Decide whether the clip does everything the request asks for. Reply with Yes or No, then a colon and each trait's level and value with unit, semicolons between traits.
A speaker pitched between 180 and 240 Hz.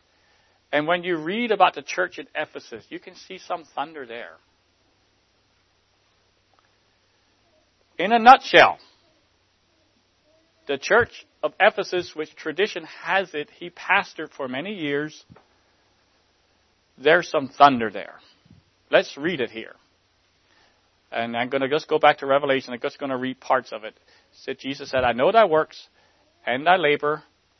No: low, 135 Hz